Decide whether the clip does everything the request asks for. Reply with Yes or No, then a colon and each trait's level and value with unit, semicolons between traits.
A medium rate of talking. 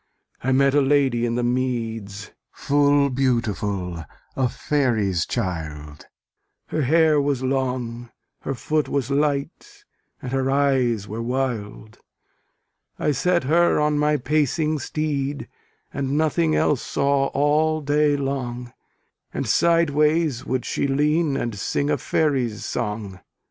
No: slow, 125 wpm